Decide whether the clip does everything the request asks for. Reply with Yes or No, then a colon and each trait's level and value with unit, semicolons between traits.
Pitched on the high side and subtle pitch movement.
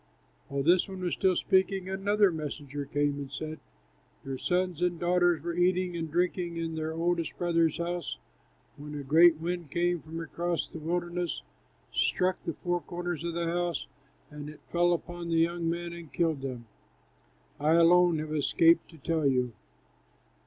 No: medium, 170 Hz; narrow, 2.0 semitones